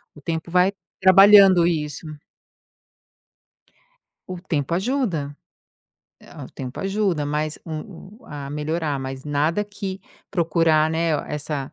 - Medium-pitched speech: Yes, medium, 165 Hz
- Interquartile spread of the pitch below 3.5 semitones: No, average, 4.0 semitones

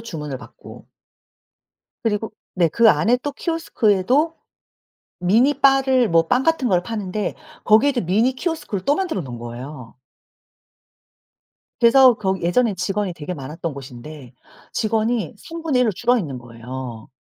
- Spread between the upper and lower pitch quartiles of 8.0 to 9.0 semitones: Yes, wide, 8.3 semitones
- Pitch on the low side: No, high, 210 Hz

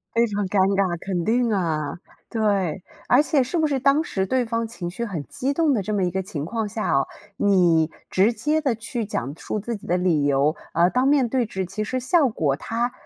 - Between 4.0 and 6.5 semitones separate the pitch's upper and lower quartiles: Yes, wide, 5.6 semitones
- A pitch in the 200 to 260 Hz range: Yes, high, 210 Hz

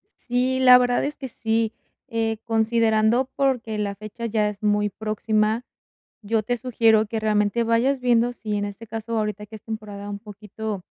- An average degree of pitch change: No, narrow, 1.9 semitones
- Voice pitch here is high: Yes, high, 220 Hz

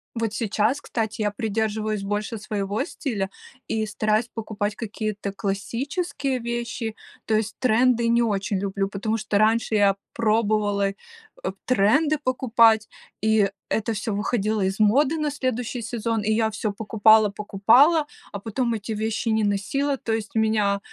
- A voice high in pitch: Yes, high, 220 Hz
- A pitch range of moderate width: No, narrow, 2.1 semitones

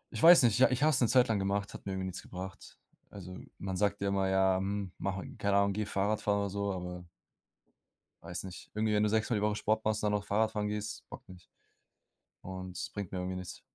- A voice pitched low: Yes, low, 100 Hz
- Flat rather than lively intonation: Yes, narrow, 2.0 semitones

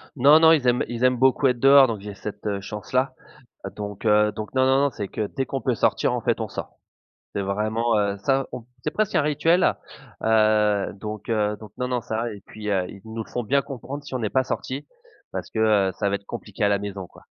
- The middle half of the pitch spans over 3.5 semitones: Yes, average, 4.1 semitones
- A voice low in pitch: Yes, low, 115 Hz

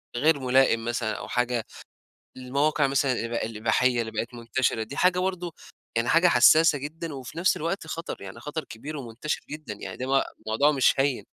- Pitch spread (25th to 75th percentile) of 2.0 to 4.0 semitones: No, average, 4.6 semitones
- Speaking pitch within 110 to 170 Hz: Yes, low, 135 Hz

